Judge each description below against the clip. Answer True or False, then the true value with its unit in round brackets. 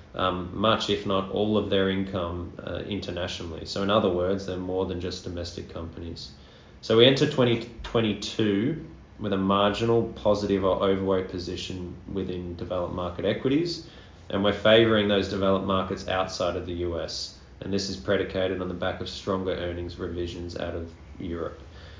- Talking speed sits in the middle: True (160 wpm)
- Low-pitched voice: True (95 Hz)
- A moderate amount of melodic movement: False (2.3 semitones)